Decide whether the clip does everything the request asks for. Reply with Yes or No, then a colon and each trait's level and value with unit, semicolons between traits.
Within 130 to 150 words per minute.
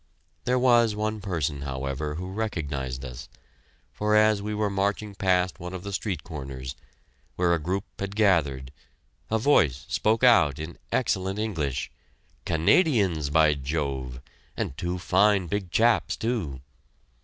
Yes: average, 140 wpm